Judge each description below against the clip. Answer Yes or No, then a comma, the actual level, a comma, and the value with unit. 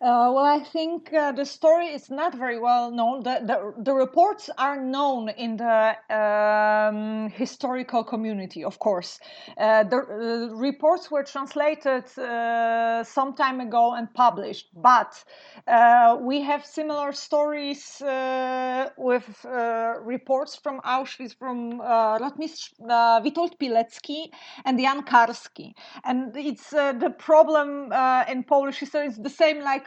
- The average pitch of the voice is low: No, very high, 260 Hz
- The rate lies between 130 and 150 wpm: Yes, average, 140 wpm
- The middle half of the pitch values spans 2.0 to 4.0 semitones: Yes, average, 3.7 semitones